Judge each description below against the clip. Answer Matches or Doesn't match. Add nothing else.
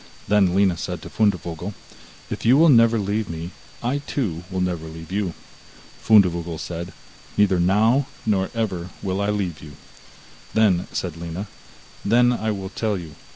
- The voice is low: Matches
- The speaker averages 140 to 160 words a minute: Matches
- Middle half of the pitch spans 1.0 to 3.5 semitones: Doesn't match